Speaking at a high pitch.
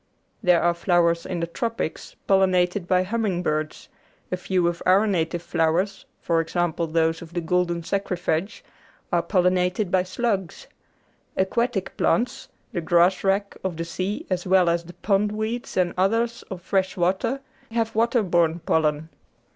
No: medium, 180 Hz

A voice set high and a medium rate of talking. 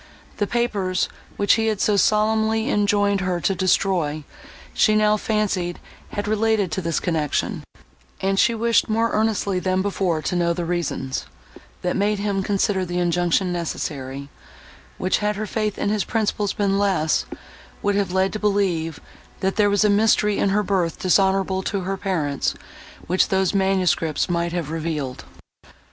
Yes: high, 195 Hz; average, 160 wpm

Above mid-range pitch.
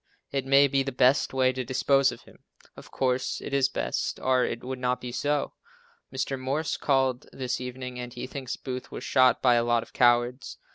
No: low, 130 Hz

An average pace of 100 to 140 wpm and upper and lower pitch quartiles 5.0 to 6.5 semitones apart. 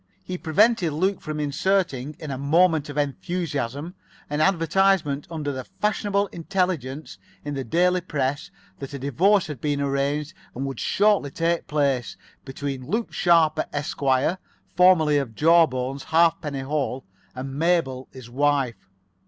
No: slow, 135 wpm; average, 4.0 semitones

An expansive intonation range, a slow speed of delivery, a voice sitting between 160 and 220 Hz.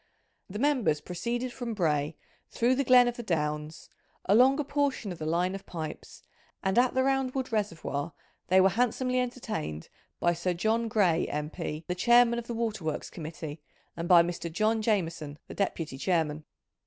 No: wide, 6.7 semitones; average, 170 wpm; high, 190 Hz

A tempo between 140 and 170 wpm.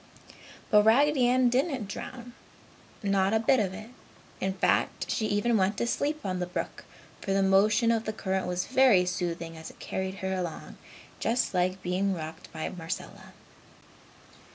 Yes: average, 165 wpm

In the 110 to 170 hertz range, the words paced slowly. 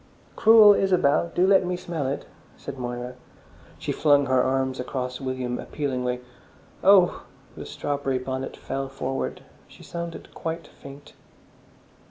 Yes: low, 135 Hz; slow, 130 wpm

